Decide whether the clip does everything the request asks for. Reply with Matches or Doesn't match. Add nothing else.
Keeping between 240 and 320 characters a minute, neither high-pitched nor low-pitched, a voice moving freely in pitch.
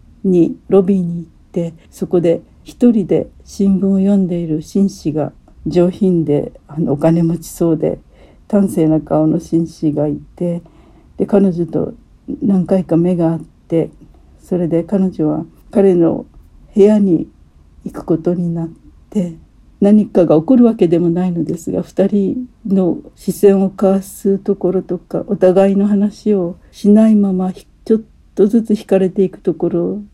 Doesn't match